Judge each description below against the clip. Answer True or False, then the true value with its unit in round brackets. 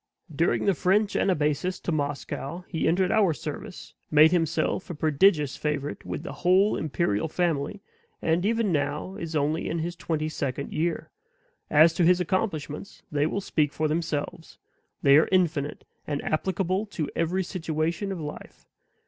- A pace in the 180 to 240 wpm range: False (155 wpm)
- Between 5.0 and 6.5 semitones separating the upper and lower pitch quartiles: False (3.5 semitones)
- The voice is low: False (165 Hz)